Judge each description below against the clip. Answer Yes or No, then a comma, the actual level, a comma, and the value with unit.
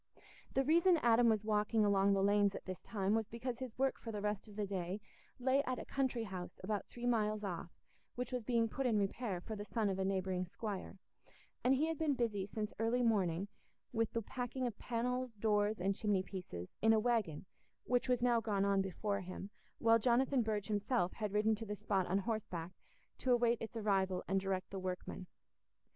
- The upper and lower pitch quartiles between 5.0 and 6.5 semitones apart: No, average, 3.5 semitones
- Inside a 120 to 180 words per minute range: No, fast, 205 wpm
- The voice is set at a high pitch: Yes, high, 215 Hz